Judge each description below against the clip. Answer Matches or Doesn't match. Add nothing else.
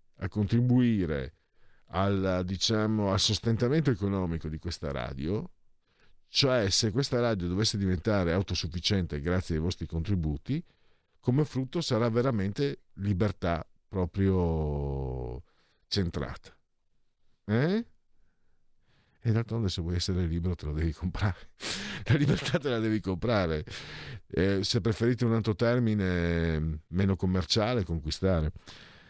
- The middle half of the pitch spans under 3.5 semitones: Doesn't match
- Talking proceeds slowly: Matches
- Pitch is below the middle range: Matches